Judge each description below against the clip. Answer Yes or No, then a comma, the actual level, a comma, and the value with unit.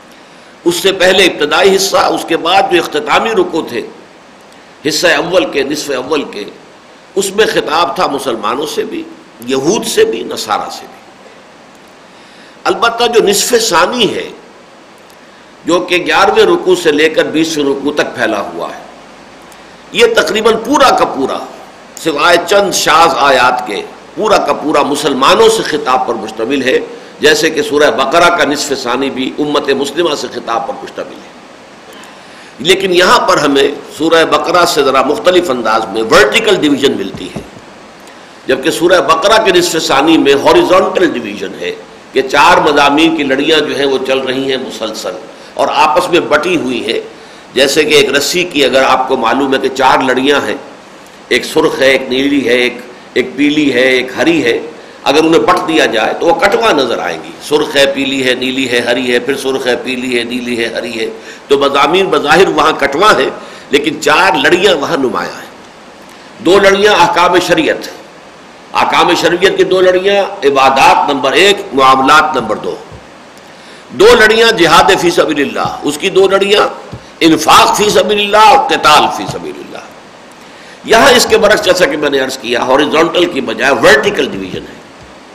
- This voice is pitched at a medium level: Yes, medium, 170 Hz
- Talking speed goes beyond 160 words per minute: Yes, average, 170 wpm